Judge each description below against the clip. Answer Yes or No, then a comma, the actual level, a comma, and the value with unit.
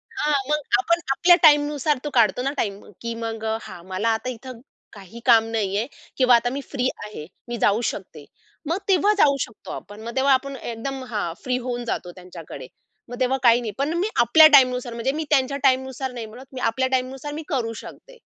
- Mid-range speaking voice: No, very high, 250 Hz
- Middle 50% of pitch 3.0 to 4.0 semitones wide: Yes, average, 3.7 semitones